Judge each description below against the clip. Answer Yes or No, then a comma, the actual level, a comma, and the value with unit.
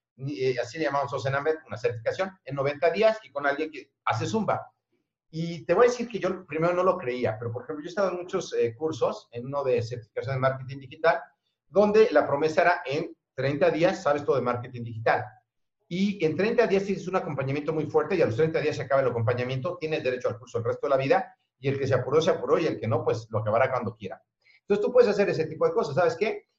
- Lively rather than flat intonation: Yes, wide, 5.8 semitones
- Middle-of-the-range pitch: Yes, medium, 155 Hz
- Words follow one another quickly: Yes, fast, 240 wpm